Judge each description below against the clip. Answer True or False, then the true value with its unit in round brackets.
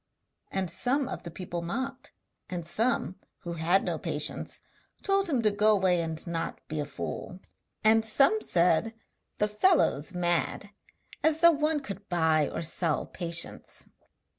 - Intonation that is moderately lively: False (6.7 semitones)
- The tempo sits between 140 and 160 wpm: True (150 wpm)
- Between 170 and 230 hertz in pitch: True (190 Hz)